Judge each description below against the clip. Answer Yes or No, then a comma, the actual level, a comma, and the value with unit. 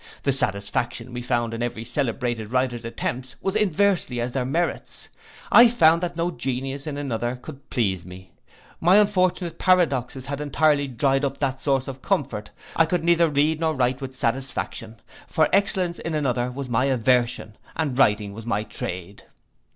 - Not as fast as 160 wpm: No, average, 165 wpm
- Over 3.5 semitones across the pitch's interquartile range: Yes, average, 4.8 semitones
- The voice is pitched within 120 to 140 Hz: Yes, low, 135 Hz